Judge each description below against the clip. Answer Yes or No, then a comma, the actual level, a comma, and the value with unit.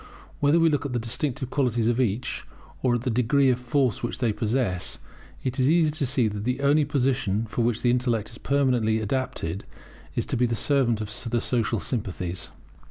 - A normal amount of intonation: Yes, average, 3.3 semitones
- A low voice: Yes, low, 125 Hz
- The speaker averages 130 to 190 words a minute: No, average, 200 wpm